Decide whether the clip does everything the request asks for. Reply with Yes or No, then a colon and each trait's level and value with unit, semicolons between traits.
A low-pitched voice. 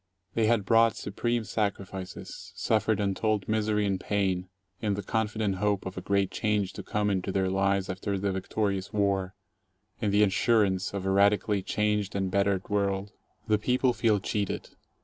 Yes: low, 100 Hz